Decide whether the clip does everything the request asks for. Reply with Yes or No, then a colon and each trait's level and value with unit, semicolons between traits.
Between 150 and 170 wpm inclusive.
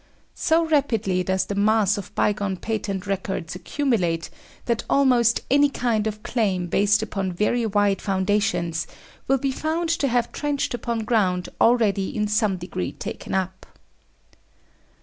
No: average, 140 wpm